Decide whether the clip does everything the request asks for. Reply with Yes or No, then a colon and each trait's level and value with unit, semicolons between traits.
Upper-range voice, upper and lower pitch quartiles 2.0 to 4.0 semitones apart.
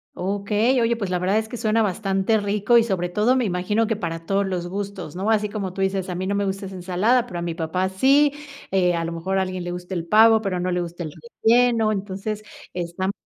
Yes: high, 195 Hz; average, 3.2 semitones